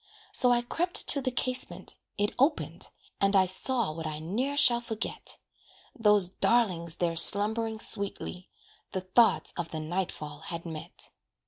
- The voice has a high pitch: Yes, high, 200 Hz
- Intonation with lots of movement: Yes, wide, 5.8 semitones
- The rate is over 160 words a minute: No, average, 150 wpm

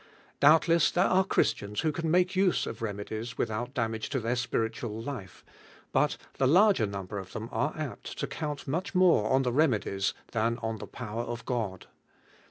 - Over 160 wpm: Yes, average, 180 wpm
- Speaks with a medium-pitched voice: No, low, 120 Hz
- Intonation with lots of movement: Yes, wide, 6.0 semitones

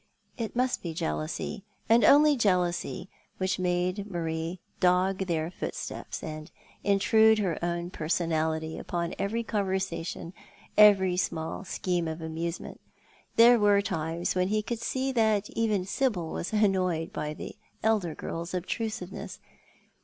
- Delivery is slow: Yes, slow, 130 wpm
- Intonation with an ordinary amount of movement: Yes, average, 3.9 semitones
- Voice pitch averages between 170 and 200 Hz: Yes, medium, 185 Hz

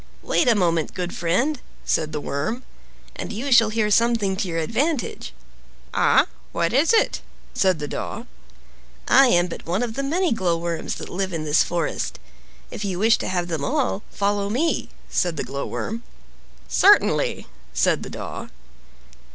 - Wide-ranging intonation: Yes, wide, 5.8 semitones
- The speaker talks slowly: No, average, 160 wpm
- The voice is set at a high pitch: Yes, high, 195 Hz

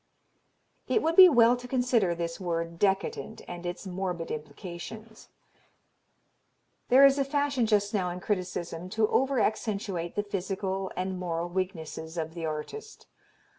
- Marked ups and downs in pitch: No, average, 4.8 semitones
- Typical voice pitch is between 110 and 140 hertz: No, high, 190 Hz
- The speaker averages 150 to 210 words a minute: No, average, 140 wpm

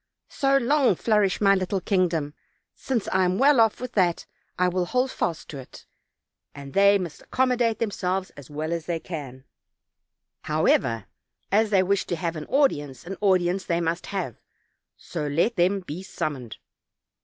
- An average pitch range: Yes, average, 4.5 semitones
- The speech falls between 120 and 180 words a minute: Yes, average, 165 wpm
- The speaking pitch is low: No, medium, 180 Hz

